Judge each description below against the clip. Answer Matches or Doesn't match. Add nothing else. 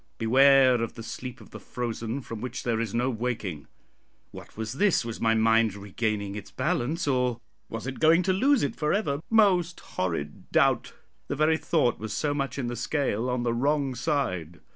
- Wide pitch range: Doesn't match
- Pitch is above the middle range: Doesn't match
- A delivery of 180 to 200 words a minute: Matches